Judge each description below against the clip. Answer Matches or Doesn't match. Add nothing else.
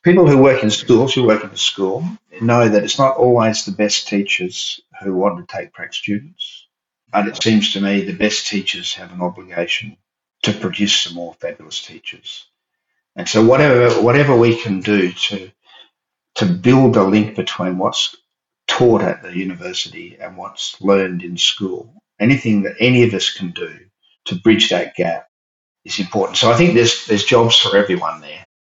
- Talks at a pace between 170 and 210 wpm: Matches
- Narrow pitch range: Doesn't match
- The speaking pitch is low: Matches